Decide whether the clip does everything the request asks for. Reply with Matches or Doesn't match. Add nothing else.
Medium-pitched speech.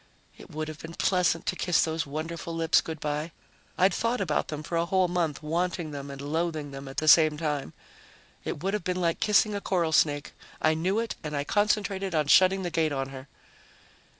Matches